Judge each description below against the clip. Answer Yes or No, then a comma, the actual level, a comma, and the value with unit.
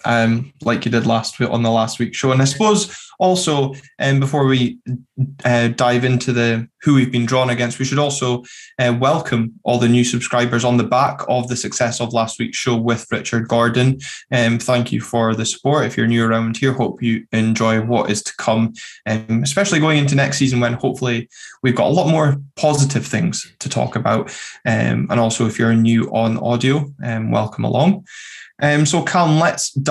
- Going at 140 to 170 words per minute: No, fast, 205 wpm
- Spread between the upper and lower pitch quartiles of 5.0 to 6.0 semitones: No, average, 2.9 semitones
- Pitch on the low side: Yes, low, 120 Hz